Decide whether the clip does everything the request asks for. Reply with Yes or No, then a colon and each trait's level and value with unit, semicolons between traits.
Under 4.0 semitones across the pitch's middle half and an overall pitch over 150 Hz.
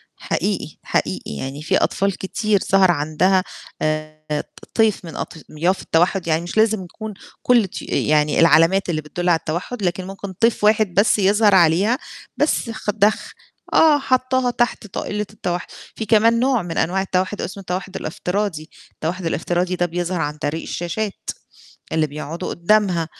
No: average, 4.3 semitones; medium, 185 Hz